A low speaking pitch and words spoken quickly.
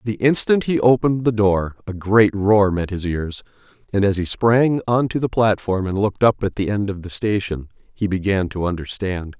Yes: low, 105 Hz; fast, 210 wpm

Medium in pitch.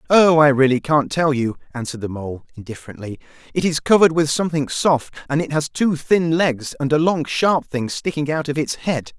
Yes: medium, 145 Hz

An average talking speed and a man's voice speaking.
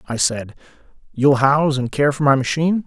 Yes: average, 190 wpm; male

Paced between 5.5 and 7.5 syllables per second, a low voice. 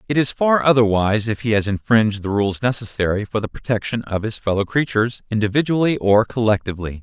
Yes: 6.2 syllables/s; low, 110 Hz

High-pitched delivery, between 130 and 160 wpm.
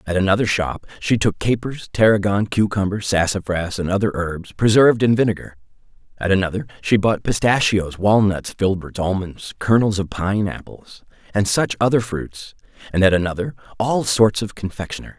No: low, 100 Hz; average, 150 wpm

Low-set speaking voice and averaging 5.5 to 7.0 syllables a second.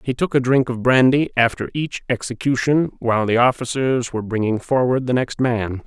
No: low, 125 Hz; 5.2 syllables/s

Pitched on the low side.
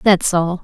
No: medium, 180 Hz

